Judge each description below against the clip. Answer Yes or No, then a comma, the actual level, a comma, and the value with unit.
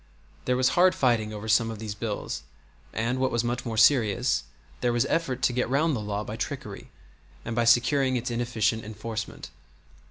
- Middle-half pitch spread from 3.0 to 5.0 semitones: No, narrow, 2.4 semitones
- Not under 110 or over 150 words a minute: No, average, 185 wpm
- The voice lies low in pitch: Yes, low, 120 Hz